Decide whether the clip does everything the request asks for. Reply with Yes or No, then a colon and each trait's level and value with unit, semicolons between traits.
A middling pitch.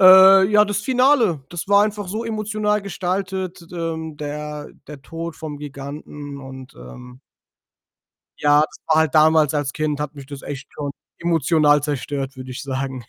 Yes: medium, 155 Hz